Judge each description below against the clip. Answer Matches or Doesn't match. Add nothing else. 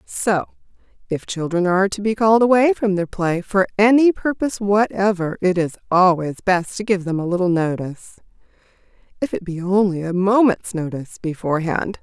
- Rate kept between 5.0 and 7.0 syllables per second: Matches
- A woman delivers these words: Matches